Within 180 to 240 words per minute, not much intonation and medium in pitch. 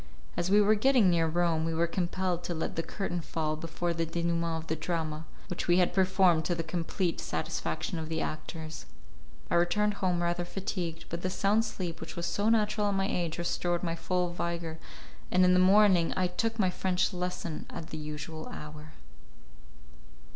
Yes: average, 190 wpm; narrow, 2.2 semitones; medium, 175 Hz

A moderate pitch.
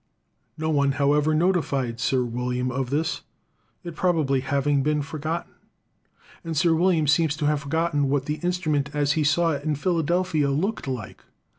Yes: medium, 150 Hz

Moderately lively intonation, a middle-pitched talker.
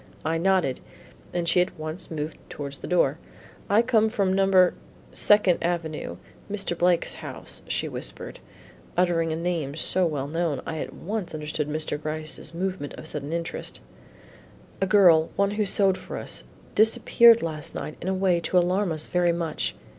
Yes: average, 3.3 semitones; medium, 170 Hz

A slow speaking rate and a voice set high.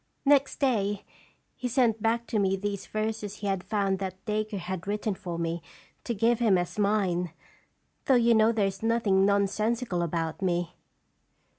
No: average, 165 wpm; high, 205 Hz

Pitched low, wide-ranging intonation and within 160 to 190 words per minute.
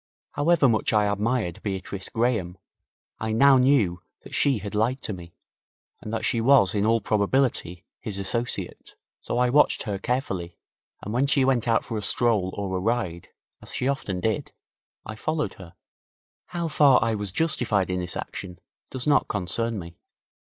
No: low, 110 Hz; average, 4.8 semitones; average, 170 wpm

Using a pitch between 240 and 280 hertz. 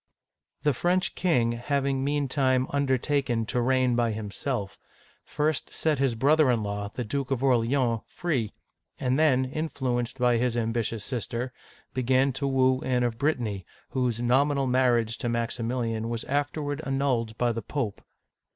No: low, 125 Hz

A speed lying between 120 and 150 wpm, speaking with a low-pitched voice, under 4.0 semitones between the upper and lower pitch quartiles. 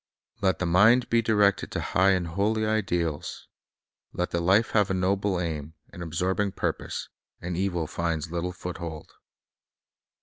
Yes: average, 145 wpm; very low, 90 Hz; average, 2.9 semitones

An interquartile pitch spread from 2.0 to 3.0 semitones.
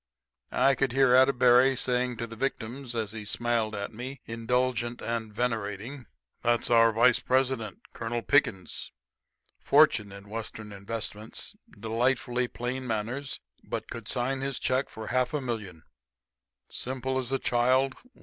Yes: narrow, 2.5 semitones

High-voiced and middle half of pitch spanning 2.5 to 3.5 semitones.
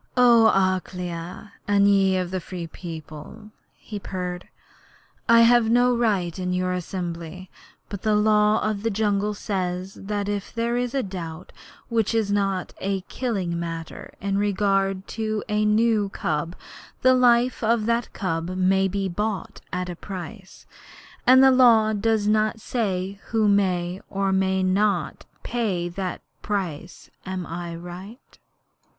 Yes: high, 195 Hz; average, 3.0 semitones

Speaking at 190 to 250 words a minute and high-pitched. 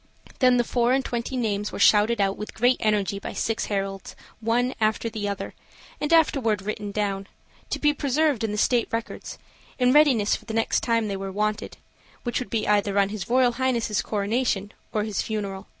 Yes: average, 195 wpm; high, 220 Hz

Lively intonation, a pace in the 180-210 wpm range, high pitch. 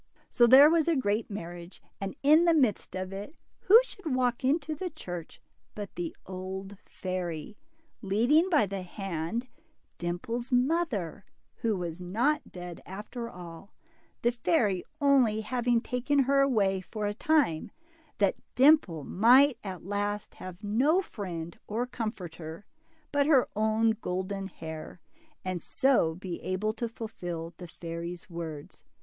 No: wide, 6.0 semitones; average, 145 wpm; high, 210 Hz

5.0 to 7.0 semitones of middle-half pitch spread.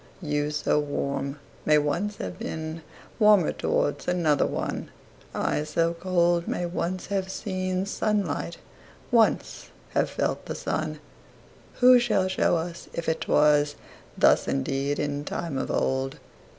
No: average, 4.2 semitones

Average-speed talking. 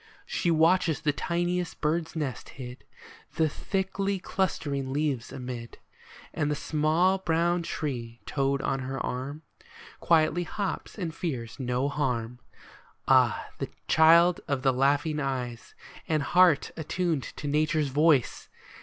No: slow, 125 wpm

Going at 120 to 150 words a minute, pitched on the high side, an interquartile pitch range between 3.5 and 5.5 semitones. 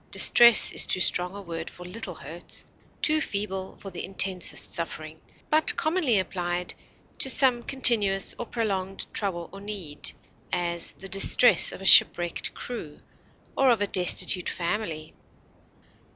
Yes: average, 140 wpm; high, 195 Hz; average, 4.4 semitones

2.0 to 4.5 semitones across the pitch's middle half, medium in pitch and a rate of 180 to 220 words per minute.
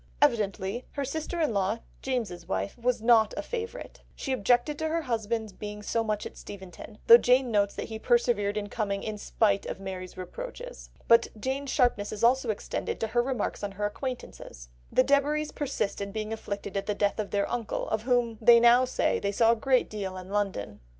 No: average, 3.7 semitones; high, 220 Hz; average, 200 wpm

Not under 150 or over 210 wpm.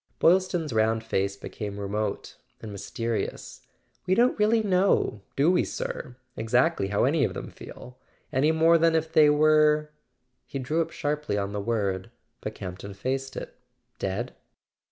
Yes: average, 155 wpm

